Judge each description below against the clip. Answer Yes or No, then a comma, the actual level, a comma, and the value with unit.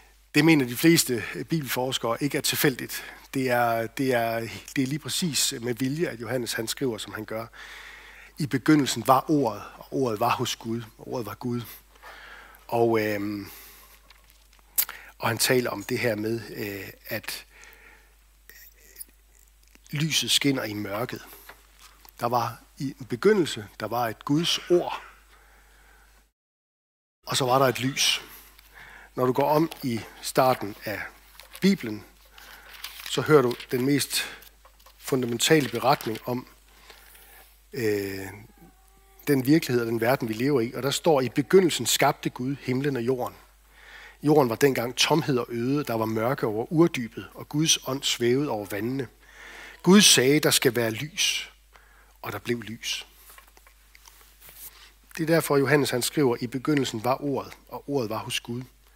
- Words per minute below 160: Yes, average, 150 wpm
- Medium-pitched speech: No, low, 130 Hz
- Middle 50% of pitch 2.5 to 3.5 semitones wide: No, average, 4.1 semitones